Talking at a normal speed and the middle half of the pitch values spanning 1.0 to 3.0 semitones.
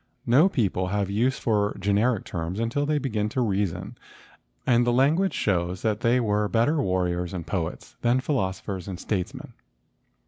No: average, 165 wpm; average, 4.8 semitones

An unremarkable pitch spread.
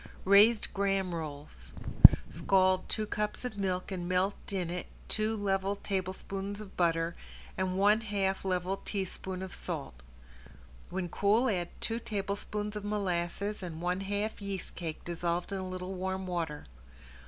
No: narrow, 2.2 semitones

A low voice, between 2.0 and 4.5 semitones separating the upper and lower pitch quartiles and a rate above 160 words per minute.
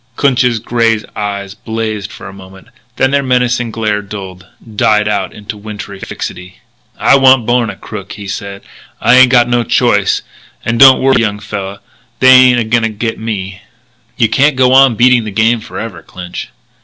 Yes: low, 110 Hz; average, 3.6 semitones; average, 180 wpm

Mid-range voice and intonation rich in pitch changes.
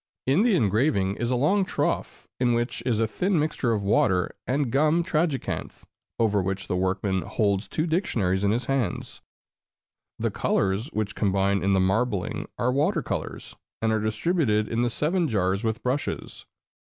No: low, 115 Hz; wide, 6.5 semitones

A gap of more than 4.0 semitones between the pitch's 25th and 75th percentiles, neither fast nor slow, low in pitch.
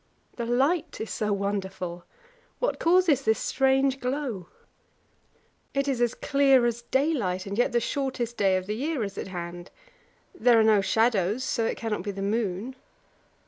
No: average, 5.1 semitones; average, 160 wpm; high, 230 Hz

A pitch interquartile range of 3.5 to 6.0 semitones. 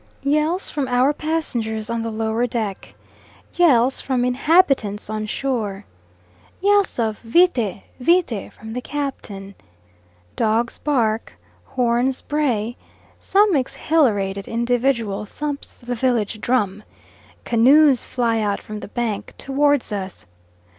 Yes: average, 4.5 semitones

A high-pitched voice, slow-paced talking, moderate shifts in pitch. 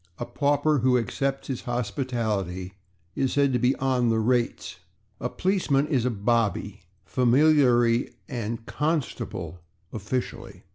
No: low, 125 Hz; slow, 125 wpm; average, 3.1 semitones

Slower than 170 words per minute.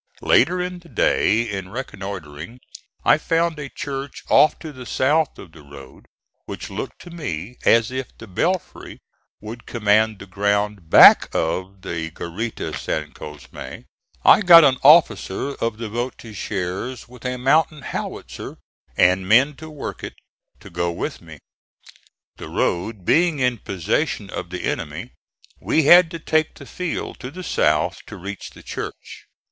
Yes: average, 155 wpm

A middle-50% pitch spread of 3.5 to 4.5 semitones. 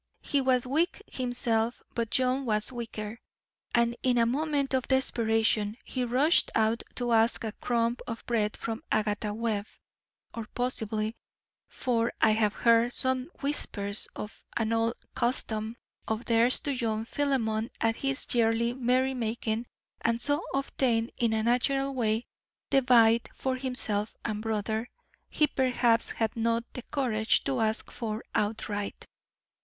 No: narrow, 2.4 semitones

